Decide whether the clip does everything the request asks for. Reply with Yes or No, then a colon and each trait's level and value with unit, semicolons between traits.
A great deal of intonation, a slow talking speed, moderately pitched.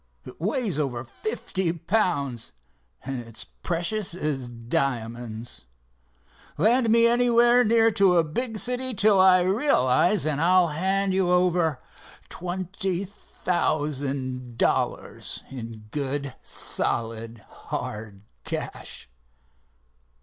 Yes: wide, 7.8 semitones; slow, 100 wpm; medium, 170 Hz